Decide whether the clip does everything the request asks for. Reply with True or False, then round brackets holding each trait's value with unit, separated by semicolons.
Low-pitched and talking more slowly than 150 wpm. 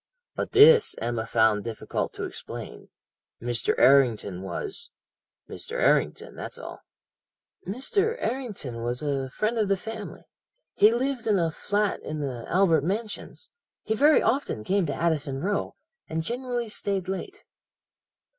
False (195 Hz; 135 wpm)